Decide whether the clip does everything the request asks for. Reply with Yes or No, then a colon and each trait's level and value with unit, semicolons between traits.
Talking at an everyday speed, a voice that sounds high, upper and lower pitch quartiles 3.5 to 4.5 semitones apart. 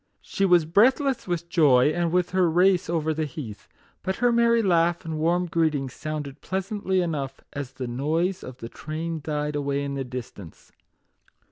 No: average, 170 wpm; medium, 160 Hz; average, 4.1 semitones